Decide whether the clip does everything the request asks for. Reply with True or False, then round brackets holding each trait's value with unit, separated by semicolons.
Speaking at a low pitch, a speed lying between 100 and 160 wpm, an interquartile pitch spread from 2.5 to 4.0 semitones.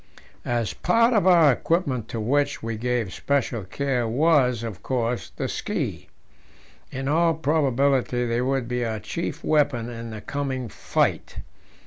True (125 Hz; 145 wpm; 3.7 semitones)